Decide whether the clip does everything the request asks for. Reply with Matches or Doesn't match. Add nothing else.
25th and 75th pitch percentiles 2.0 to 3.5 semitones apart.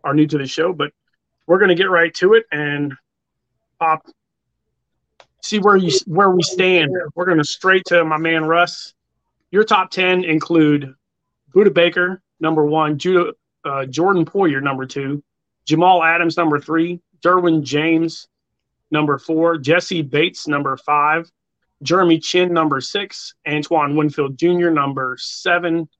Matches